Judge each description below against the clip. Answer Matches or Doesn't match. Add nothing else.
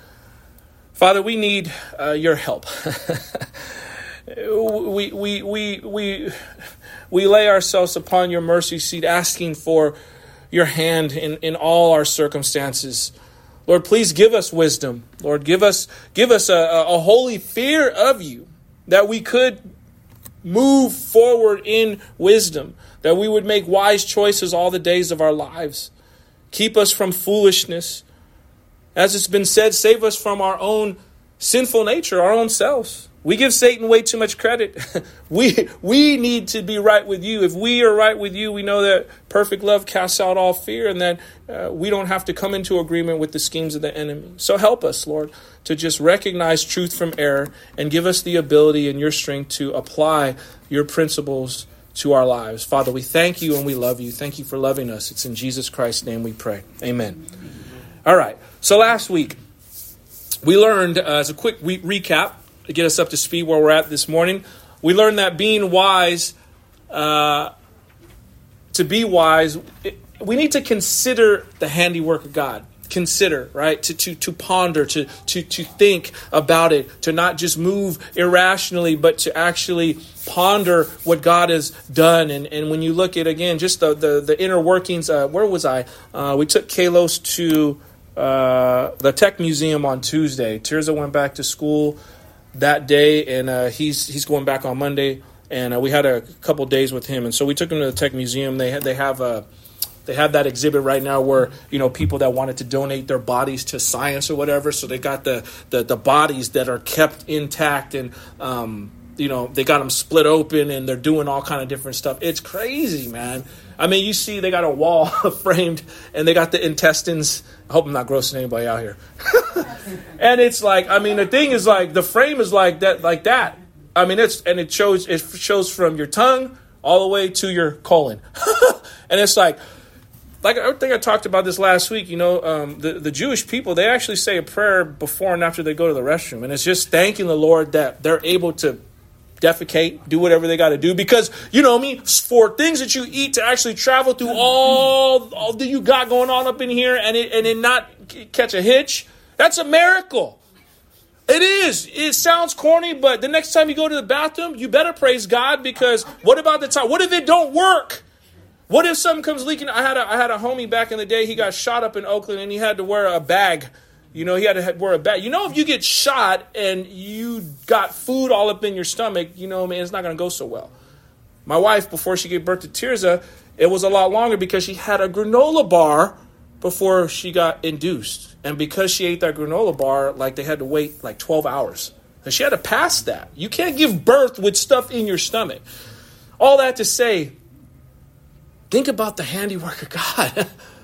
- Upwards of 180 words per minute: Matches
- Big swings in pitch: Matches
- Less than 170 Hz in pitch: Doesn't match